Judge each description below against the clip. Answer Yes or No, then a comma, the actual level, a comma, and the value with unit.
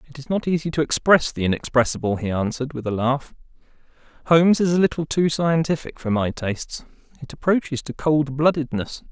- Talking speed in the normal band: Yes, average, 170 wpm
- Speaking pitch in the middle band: Yes, medium, 145 Hz